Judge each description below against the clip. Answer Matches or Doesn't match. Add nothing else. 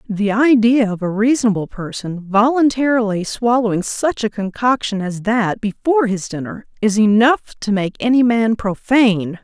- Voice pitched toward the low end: Doesn't match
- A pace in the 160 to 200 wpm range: Doesn't match